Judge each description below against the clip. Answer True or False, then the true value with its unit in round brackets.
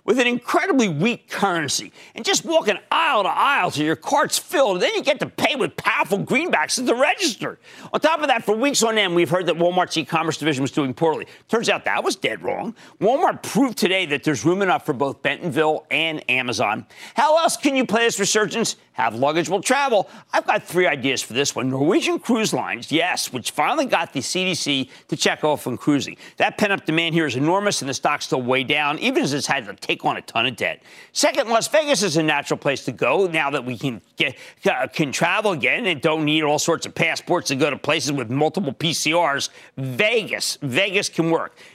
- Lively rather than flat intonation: True (6.5 semitones)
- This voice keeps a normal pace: False (220 wpm)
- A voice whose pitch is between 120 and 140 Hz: False (165 Hz)